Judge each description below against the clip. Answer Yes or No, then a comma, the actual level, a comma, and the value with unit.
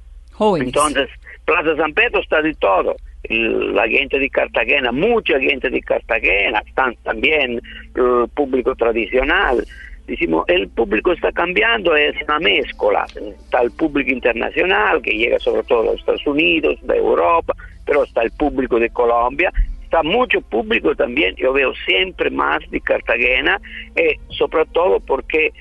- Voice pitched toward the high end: Yes, very high, 330 Hz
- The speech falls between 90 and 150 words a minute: Yes, average, 140 wpm